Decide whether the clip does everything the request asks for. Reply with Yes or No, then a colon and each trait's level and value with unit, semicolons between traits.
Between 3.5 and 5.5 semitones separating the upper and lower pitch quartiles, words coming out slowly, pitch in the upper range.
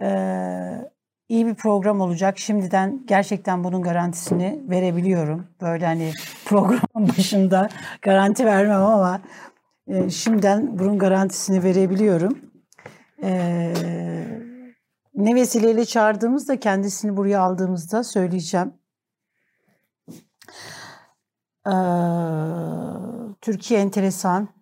No: average, 3.1 semitones; slow, 80 wpm; high, 195 Hz